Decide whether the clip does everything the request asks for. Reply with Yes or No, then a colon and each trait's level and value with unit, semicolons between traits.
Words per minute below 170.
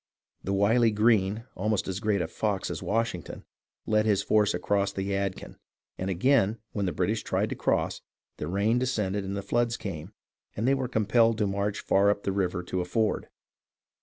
No: average, 190 wpm